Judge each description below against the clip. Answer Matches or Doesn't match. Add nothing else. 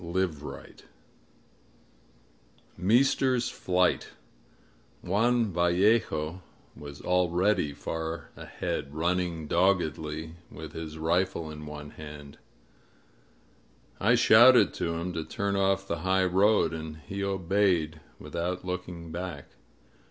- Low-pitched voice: Matches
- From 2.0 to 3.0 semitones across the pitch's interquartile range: Doesn't match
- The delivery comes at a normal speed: Doesn't match